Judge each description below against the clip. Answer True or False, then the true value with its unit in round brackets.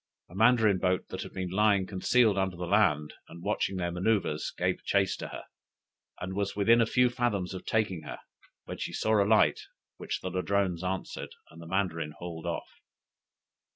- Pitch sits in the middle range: False (95 Hz)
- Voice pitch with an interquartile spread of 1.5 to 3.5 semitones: True (3.1 semitones)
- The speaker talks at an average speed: True (185 wpm)